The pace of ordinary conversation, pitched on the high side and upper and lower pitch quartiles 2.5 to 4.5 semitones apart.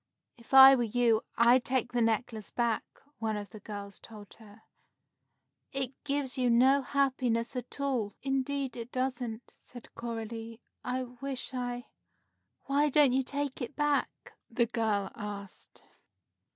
Yes: average, 145 wpm; high, 245 Hz; average, 2.9 semitones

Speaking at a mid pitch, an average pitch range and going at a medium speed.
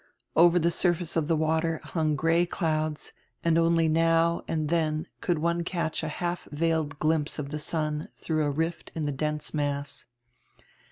No: medium, 160 Hz; narrow, 1.6 semitones; average, 170 wpm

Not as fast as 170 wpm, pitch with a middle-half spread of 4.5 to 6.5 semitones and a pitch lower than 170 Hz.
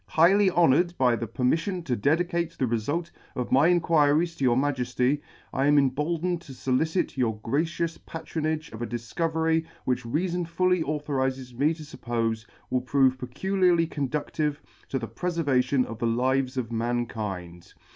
Yes: average, 155 wpm; average, 4.8 semitones; medium, 140 Hz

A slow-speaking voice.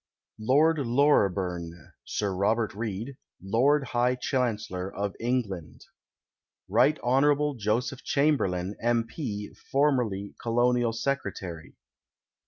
Yes: slow, 95 wpm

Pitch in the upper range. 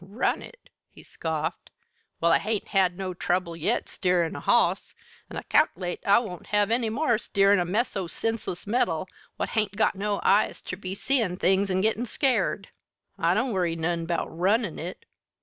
Yes: high, 195 Hz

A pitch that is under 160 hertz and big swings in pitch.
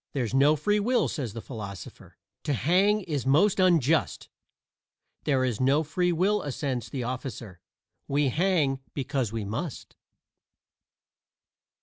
Yes: medium, 140 Hz; wide, 5.9 semitones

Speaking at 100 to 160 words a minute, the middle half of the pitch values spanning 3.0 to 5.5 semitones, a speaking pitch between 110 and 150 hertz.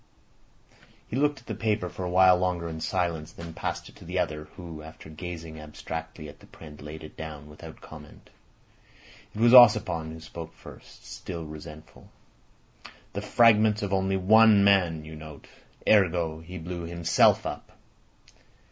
No: average, 155 wpm; average, 3.3 semitones; very low, 85 Hz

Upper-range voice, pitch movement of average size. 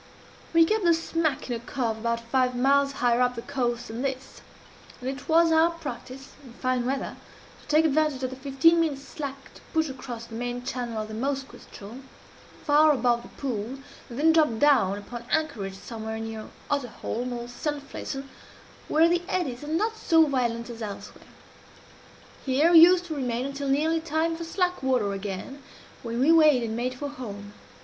Yes: very high, 265 Hz; average, 4.6 semitones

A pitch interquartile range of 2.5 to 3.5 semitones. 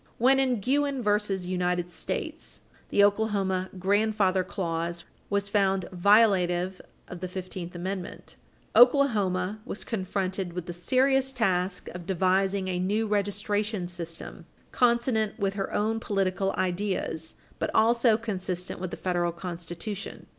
Yes: average, 3.1 semitones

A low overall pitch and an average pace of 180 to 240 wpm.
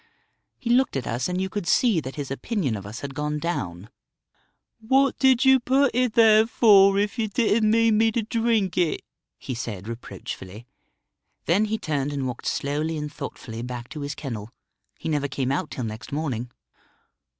No: medium, 160 Hz; average, 185 wpm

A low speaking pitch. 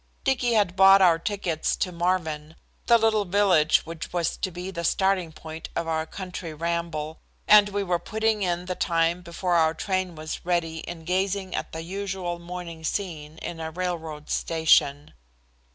No: medium, 175 Hz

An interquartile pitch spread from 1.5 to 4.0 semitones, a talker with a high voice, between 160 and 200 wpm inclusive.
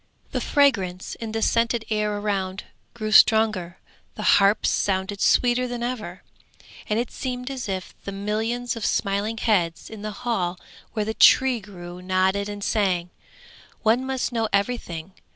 No: average, 3.6 semitones; high, 210 Hz; average, 150 wpm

